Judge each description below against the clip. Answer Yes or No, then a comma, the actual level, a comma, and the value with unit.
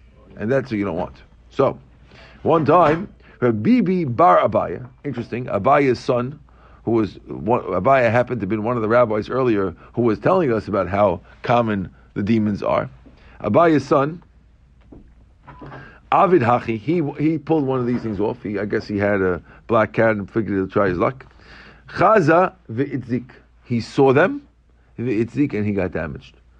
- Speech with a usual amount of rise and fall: Yes, average, 4.0 semitones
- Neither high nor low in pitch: No, low, 115 Hz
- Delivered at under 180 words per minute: Yes, average, 165 wpm